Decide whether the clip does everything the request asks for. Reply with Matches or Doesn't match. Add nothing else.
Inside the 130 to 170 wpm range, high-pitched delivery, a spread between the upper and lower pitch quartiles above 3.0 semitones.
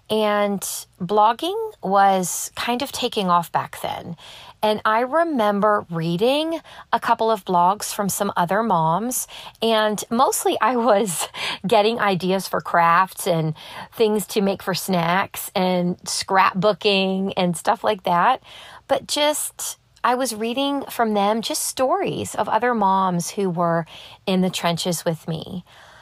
Matches